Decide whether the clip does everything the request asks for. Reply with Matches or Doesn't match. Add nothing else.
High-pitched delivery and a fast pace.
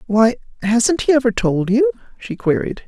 Doesn't match